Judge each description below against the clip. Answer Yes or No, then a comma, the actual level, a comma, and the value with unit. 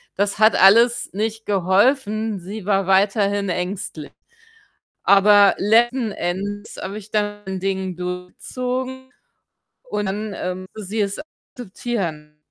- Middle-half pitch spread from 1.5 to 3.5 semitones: Yes, narrow, 2.5 semitones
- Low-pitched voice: No, high, 205 Hz